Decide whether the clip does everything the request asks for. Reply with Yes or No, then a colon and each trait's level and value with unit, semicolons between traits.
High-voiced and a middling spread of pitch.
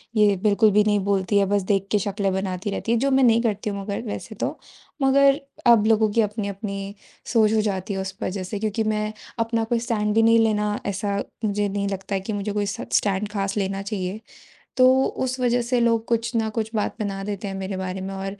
No: high, 210 Hz; narrow, 2.3 semitones